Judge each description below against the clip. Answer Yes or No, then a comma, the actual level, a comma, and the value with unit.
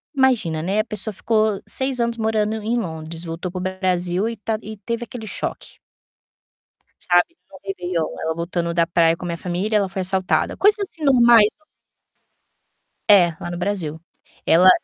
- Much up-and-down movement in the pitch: No, average, 4.2 semitones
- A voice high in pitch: Yes, high, 195 Hz